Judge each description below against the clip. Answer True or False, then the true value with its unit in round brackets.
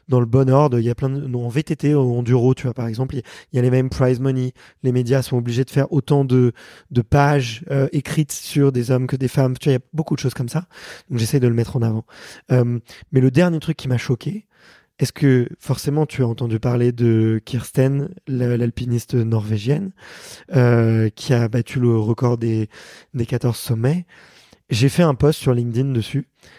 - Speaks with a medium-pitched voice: False (130 Hz)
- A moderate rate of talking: False (225 wpm)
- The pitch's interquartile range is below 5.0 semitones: True (2.8 semitones)